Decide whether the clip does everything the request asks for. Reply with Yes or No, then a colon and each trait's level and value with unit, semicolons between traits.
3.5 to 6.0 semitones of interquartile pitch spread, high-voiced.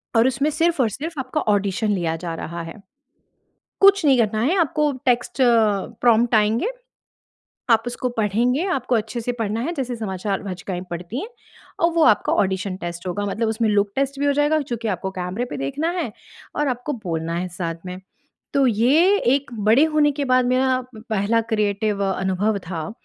Yes: wide, 5.4 semitones; high, 225 Hz